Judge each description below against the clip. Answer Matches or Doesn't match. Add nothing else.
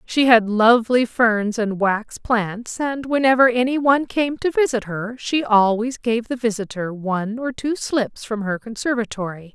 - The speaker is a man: Doesn't match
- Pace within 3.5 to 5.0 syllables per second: Matches